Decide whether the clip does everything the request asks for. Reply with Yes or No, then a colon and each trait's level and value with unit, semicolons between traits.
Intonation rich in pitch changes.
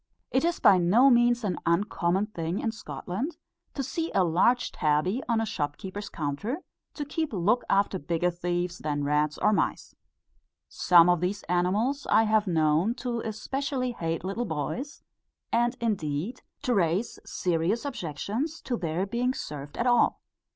Yes: wide, 6.1 semitones